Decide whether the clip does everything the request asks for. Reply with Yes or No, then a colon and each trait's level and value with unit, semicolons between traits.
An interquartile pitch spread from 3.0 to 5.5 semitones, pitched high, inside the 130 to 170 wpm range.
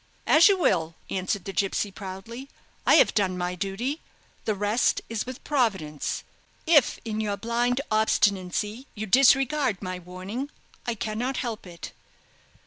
Yes: average, 4.7 semitones; high, 215 Hz; average, 140 wpm